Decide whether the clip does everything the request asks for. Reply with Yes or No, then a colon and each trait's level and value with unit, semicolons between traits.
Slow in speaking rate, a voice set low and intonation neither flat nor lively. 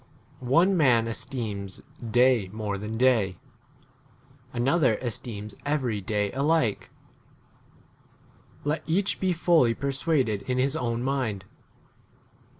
Yes: slow, 100 wpm; low, 125 Hz; average, 4.7 semitones